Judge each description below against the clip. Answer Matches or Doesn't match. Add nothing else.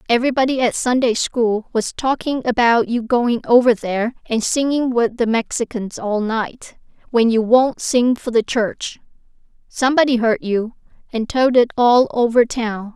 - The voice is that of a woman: Matches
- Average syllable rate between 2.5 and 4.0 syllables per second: Doesn't match